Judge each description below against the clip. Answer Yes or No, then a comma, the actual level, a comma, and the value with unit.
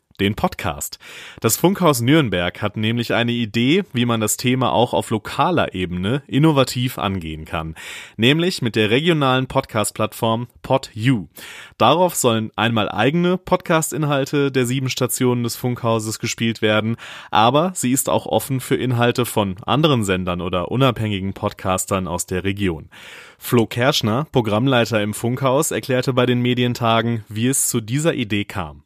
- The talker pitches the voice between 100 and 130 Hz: Yes, low, 120 Hz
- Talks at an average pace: Yes, average, 145 wpm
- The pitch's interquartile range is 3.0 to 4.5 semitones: Yes, average, 3.8 semitones